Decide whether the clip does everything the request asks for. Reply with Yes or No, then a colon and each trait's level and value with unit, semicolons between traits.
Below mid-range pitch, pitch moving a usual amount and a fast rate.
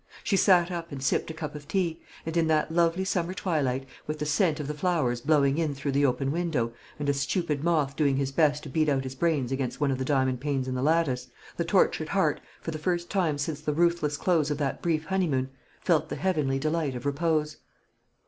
No: medium, 150 Hz; average, 3.4 semitones; fast, 225 wpm